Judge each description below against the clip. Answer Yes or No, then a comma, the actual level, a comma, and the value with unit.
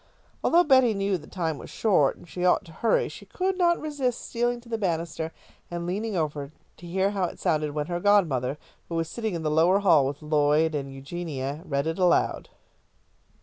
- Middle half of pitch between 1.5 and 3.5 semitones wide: No, average, 5.2 semitones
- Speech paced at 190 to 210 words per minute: Yes, average, 200 wpm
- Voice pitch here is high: No, medium, 175 Hz